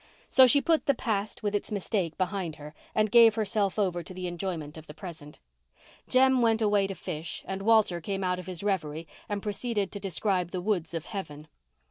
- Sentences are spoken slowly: No, average, 195 wpm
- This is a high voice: Yes, high, 195 Hz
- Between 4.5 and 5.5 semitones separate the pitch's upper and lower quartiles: No, average, 3.7 semitones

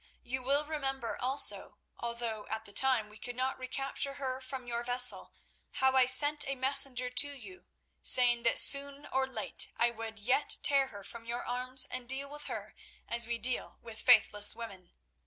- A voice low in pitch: No, very high, 255 Hz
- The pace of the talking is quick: No, average, 180 wpm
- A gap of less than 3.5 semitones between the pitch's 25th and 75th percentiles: Yes, narrow, 2.4 semitones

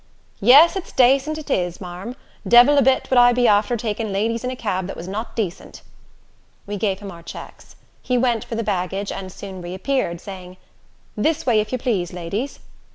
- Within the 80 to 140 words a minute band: No, average, 195 wpm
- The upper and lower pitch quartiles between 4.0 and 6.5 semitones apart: Yes, average, 4.8 semitones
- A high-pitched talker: Yes, high, 215 Hz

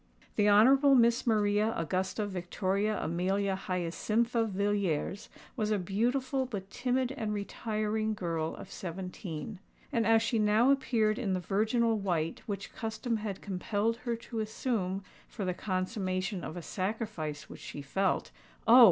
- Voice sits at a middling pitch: No, high, 210 Hz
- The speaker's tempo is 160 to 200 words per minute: No, slow, 135 wpm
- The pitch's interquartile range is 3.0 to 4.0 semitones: Yes, average, 3.4 semitones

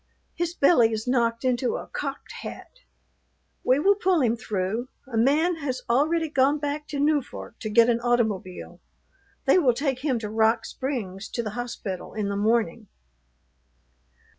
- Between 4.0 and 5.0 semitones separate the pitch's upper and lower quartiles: Yes, average, 4.4 semitones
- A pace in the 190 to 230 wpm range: No, average, 160 wpm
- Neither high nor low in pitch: No, high, 245 Hz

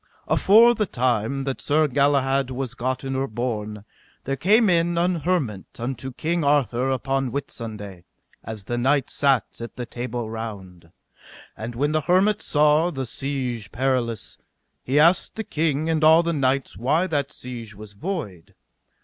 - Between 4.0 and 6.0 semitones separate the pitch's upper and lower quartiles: Yes, average, 4.8 semitones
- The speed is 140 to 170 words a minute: Yes, average, 155 wpm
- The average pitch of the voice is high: No, low, 135 Hz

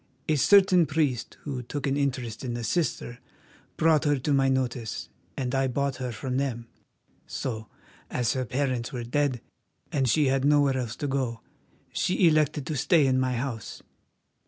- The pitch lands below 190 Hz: Yes, low, 135 Hz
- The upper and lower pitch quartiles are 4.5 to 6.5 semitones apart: No, average, 2.8 semitones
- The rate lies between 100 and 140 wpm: No, average, 170 wpm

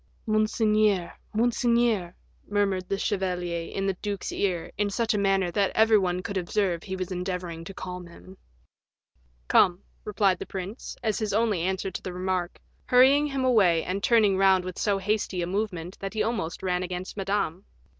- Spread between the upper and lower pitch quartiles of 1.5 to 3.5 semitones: Yes, average, 2.8 semitones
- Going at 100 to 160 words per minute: No, average, 175 wpm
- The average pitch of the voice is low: No, high, 195 Hz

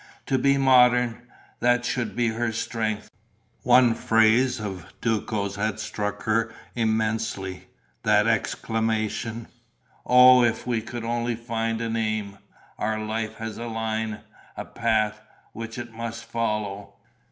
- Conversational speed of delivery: No, slow, 130 wpm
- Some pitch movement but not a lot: No, narrow, 1.5 semitones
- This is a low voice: Yes, low, 115 Hz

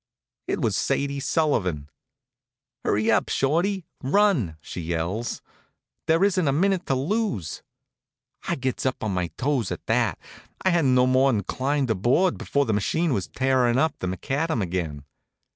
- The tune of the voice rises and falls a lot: Yes, wide, 7.6 semitones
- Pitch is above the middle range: No, low, 130 Hz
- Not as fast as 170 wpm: Yes, average, 155 wpm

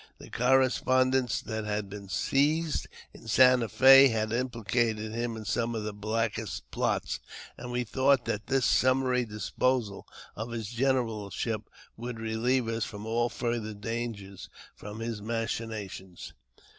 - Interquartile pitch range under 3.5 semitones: Yes, average, 2.7 semitones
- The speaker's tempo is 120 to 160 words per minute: Yes, average, 140 wpm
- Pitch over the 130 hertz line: No, low, 115 Hz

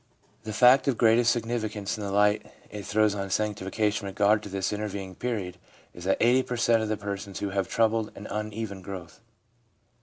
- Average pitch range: No, narrow, 2.3 semitones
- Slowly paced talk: No, average, 190 wpm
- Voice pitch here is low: Yes, low, 105 Hz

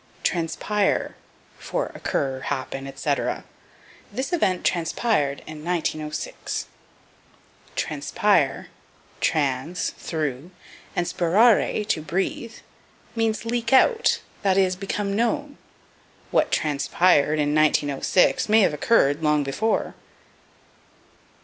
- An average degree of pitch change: No, wide, 6.5 semitones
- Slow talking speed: Yes, slow, 90 wpm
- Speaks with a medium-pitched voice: Yes, medium, 170 Hz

